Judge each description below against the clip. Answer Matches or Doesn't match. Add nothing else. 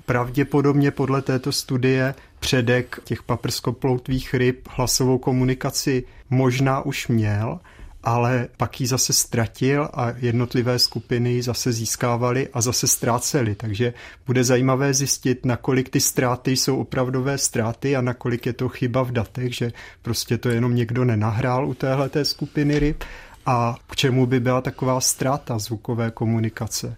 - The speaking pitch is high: Doesn't match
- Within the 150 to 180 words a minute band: Doesn't match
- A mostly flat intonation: Matches